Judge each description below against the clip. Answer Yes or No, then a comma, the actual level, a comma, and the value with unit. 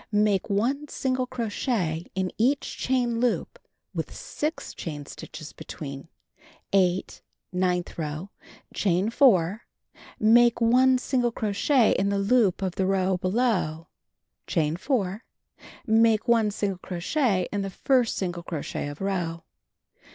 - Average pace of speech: No, slow, 125 wpm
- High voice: Yes, high, 200 Hz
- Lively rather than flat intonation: No, average, 5.0 semitones